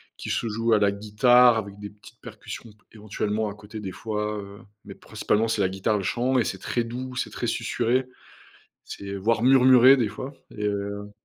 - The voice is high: No, low, 110 Hz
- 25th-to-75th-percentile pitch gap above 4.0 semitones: No, average, 2.9 semitones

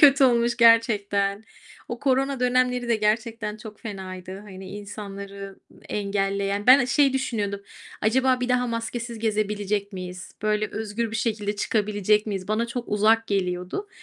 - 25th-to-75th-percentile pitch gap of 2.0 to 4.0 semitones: Yes, average, 2.9 semitones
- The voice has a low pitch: No, high, 215 Hz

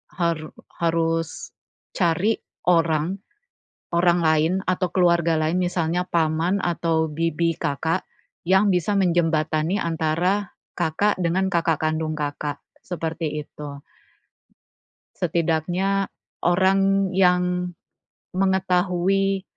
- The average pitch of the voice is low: No, medium, 170 Hz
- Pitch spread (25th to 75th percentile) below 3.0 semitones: Yes, narrow, 2.5 semitones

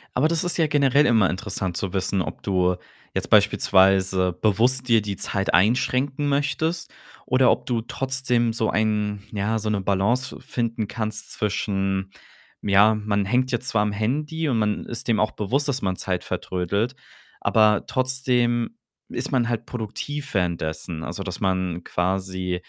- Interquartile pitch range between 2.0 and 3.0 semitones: No, average, 4.7 semitones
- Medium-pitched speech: No, low, 110 Hz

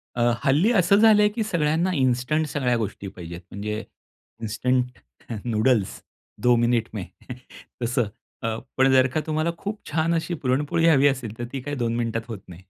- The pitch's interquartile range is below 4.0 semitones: No, wide, 5.4 semitones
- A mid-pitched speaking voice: No, low, 130 Hz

